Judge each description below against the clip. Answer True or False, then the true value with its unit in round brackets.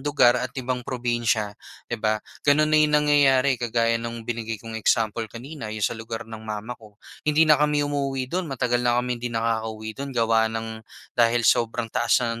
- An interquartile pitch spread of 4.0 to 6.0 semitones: False (3.0 semitones)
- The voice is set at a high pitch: False (120 Hz)